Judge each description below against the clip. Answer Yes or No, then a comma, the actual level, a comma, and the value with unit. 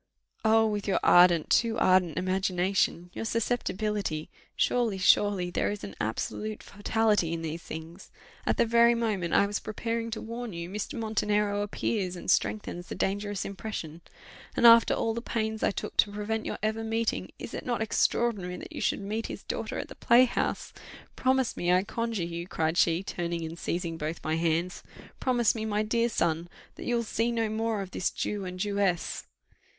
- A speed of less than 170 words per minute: No, average, 185 wpm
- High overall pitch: Yes, high, 205 Hz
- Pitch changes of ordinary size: Yes, average, 4.1 semitones